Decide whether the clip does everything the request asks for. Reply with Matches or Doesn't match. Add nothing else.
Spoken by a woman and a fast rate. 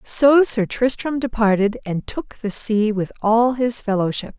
Doesn't match